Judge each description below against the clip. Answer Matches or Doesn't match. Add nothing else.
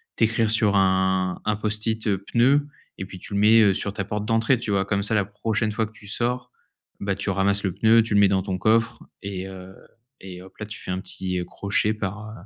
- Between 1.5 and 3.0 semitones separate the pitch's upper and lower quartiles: Matches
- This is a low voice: Matches